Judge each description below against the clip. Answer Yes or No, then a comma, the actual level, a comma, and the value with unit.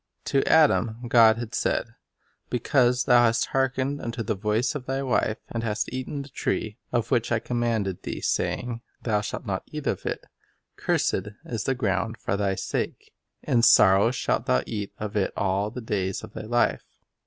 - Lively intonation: No, average, 3.0 semitones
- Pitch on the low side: Yes, low, 115 Hz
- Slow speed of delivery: No, average, 190 wpm